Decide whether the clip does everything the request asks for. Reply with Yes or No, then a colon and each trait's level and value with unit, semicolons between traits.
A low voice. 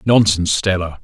Yes: very low, 95 Hz